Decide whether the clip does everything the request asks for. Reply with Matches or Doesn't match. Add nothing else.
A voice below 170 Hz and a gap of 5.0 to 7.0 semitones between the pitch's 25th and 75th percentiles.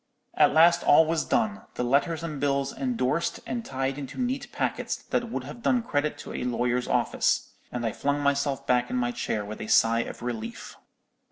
Matches